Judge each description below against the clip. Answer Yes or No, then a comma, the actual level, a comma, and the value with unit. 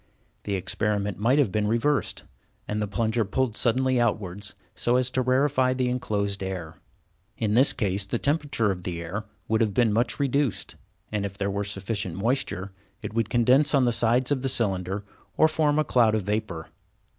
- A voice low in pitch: Yes, low, 110 Hz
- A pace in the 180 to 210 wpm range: Yes, average, 185 wpm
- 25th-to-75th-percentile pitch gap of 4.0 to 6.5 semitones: Yes, average, 4.3 semitones